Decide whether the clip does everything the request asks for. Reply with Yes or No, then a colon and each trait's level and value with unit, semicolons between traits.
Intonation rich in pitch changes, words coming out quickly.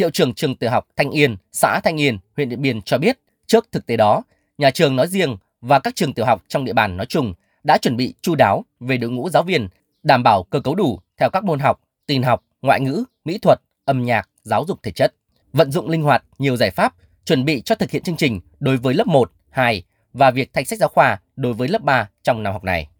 No: average, 4.8 semitones; fast, 255 wpm